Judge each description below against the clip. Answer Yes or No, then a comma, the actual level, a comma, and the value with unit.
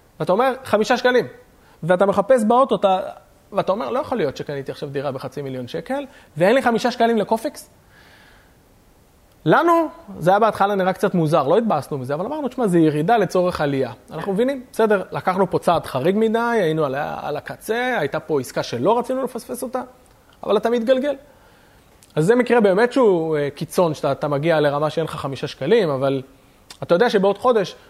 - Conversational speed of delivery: No, fast, 180 wpm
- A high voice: Yes, high, 195 Hz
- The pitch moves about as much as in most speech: No, wide, 8.2 semitones